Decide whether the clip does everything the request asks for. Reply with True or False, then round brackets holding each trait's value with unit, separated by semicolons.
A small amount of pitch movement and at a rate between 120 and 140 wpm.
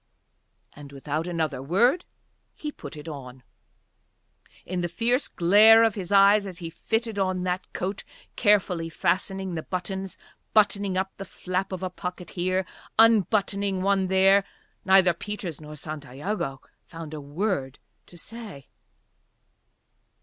False (3.4 semitones; 135 wpm)